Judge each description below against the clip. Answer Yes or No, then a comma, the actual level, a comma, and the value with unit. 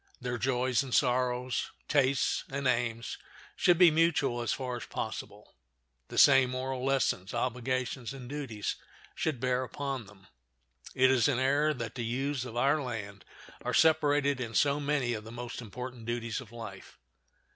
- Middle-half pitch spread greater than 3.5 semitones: No, narrow, 2.5 semitones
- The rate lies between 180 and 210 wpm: No, average, 160 wpm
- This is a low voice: Yes, low, 130 Hz